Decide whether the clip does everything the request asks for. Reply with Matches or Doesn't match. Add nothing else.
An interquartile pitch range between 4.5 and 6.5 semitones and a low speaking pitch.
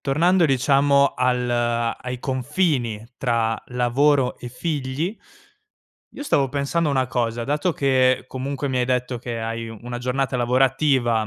Doesn't match